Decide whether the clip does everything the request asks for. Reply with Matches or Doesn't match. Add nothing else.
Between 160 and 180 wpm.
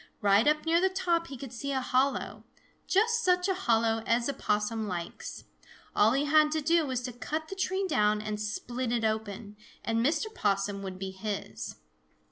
Doesn't match